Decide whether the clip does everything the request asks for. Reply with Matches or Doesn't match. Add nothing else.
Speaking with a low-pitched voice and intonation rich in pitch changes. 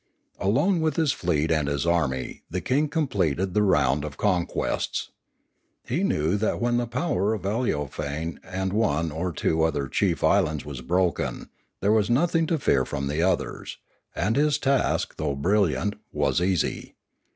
Matches